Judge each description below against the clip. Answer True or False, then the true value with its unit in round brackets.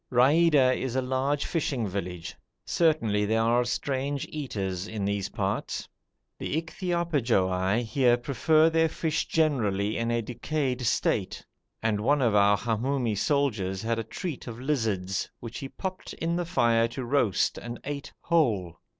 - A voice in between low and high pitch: False (120 Hz)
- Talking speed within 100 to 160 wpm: True (150 wpm)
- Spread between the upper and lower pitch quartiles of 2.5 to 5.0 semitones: False (5.5 semitones)